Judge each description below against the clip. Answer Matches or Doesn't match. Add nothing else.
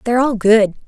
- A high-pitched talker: Matches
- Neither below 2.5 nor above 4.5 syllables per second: Doesn't match